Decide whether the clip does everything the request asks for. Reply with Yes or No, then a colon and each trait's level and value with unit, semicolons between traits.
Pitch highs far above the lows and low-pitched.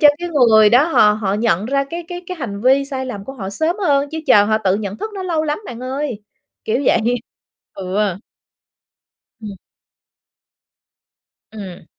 No: wide, 6.2 semitones; very high, 250 Hz